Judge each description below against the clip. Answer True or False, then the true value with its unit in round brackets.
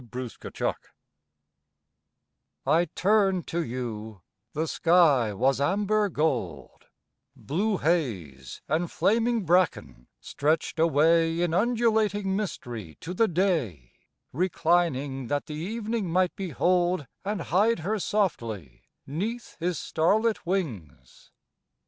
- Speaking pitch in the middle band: True (170 Hz)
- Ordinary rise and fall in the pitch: False (6.5 semitones)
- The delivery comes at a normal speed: False (105 wpm)